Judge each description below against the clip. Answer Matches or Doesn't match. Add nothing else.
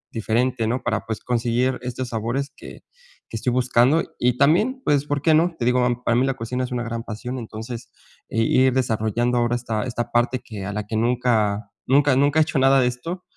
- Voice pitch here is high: Doesn't match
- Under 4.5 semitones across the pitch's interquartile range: Matches